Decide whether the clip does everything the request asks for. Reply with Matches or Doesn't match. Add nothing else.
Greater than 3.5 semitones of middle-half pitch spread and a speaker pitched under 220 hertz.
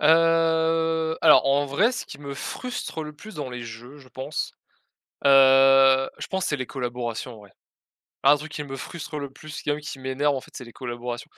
Doesn't match